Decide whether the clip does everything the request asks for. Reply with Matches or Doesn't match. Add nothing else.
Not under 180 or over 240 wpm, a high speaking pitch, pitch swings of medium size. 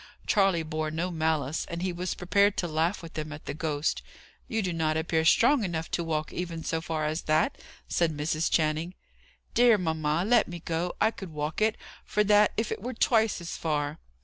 Doesn't match